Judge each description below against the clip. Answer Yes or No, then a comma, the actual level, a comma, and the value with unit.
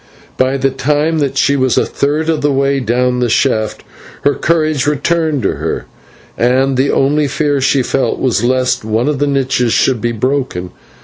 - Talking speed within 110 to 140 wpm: No, average, 185 wpm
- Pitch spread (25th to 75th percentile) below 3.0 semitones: Yes, narrow, 2.5 semitones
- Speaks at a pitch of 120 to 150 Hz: Yes, low, 135 Hz